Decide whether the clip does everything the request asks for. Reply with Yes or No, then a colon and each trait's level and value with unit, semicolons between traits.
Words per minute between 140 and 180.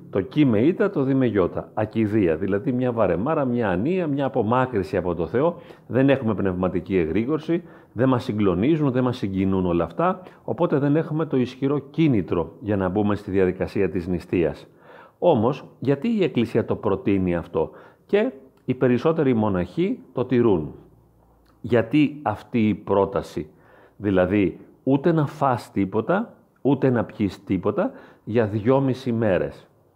Yes: average, 145 wpm